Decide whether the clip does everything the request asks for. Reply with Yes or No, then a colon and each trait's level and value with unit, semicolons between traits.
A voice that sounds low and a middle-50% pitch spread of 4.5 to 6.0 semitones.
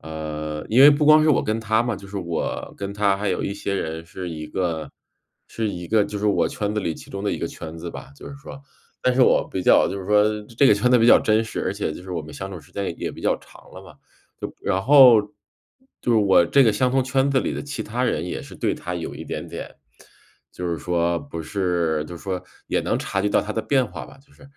Yes: low, 100 Hz; wide, 5.5 semitones